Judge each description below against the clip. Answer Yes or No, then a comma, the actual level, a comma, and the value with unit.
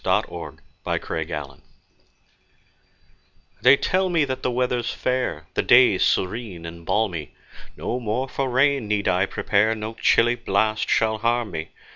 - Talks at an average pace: Yes, average, 145 wpm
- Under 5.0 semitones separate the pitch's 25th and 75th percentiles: No, average, 5.3 semitones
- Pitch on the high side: No, low, 110 Hz